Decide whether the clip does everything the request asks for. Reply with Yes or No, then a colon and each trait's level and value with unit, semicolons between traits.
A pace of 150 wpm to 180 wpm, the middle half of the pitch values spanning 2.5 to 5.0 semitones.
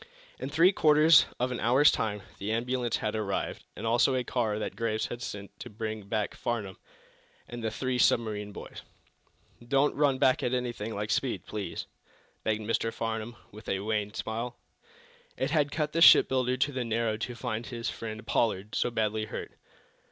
Yes: average, 175 wpm; average, 2.9 semitones